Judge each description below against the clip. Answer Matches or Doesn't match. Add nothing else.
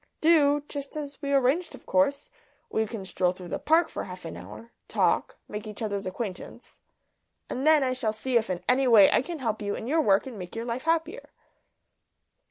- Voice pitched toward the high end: Matches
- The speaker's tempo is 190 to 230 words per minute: Matches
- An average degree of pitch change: Doesn't match